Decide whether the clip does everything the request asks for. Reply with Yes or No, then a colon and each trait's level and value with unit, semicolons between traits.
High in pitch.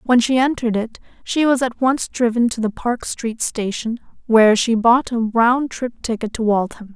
Yes: high, 235 Hz